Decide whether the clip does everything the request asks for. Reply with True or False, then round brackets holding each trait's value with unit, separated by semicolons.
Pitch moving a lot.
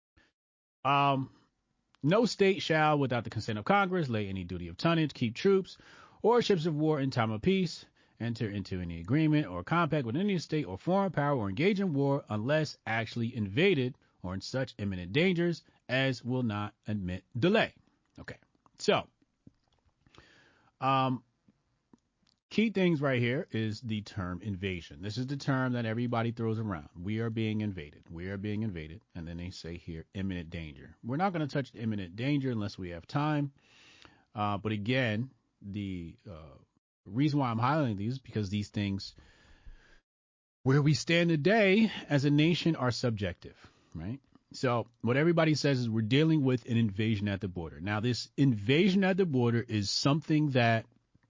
True (6.2 semitones)